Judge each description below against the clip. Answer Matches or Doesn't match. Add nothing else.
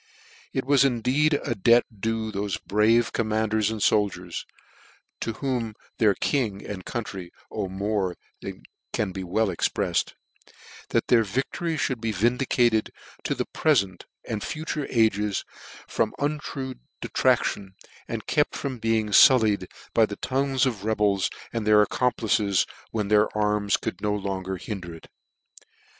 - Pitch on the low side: Matches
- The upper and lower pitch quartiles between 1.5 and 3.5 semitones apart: Matches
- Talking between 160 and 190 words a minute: Doesn't match